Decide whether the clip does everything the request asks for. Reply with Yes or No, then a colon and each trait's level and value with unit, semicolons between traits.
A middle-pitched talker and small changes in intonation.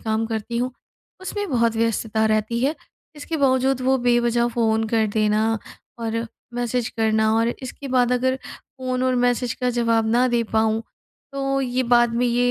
No: high, 240 Hz; narrow, 2.2 semitones